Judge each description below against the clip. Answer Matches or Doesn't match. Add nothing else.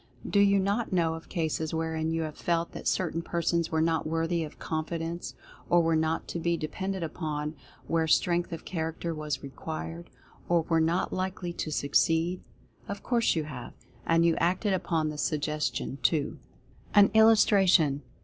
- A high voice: Doesn't match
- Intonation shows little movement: Matches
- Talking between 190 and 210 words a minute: Doesn't match